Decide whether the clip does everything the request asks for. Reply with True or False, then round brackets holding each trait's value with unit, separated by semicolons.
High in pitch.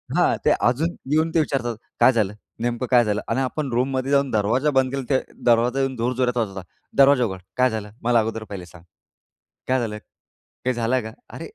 False (125 Hz)